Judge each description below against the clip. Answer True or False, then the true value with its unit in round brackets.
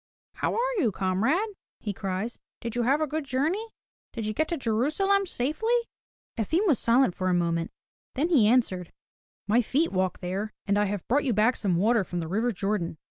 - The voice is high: True (230 Hz)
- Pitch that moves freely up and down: True (7.3 semitones)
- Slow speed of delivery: False (195 wpm)